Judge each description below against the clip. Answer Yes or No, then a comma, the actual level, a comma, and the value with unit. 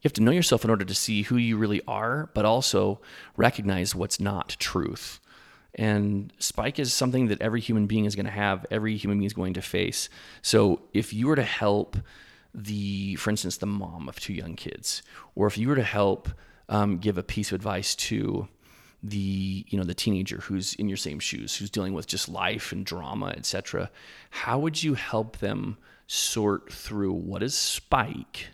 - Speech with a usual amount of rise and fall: No, narrow, 2.2 semitones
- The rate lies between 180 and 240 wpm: Yes, average, 200 wpm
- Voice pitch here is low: Yes, low, 105 Hz